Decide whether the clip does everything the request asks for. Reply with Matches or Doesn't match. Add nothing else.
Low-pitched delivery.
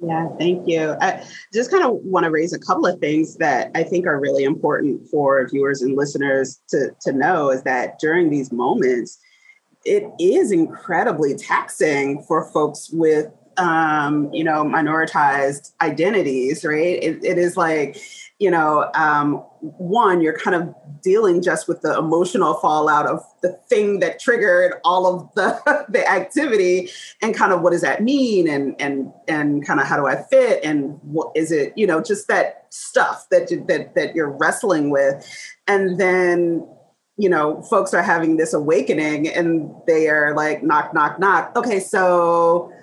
Doesn't match